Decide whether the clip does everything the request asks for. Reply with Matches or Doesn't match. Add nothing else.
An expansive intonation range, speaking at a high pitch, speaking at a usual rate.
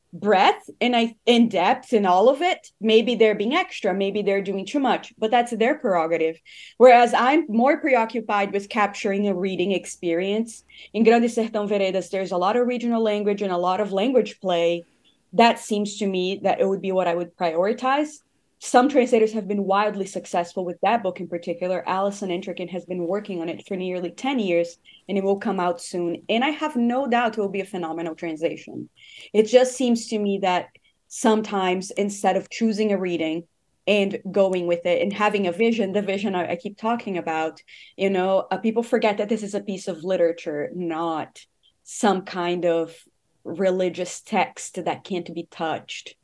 Doesn't match